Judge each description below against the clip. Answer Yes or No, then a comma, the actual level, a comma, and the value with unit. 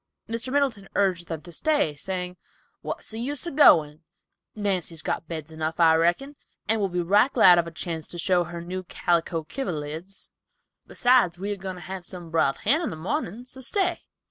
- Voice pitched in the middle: Yes, medium, 180 Hz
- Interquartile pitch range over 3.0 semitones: Yes, average, 5.1 semitones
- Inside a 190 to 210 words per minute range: Yes, average, 195 wpm